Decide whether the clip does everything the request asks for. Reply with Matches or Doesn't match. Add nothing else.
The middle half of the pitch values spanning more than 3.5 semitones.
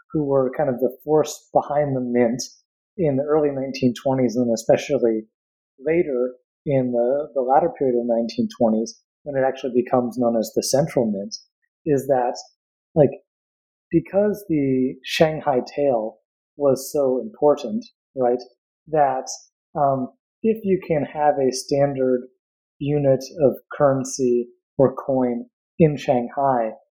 Doesn't match